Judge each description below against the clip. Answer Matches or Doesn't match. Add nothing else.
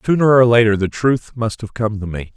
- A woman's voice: Doesn't match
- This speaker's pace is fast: Matches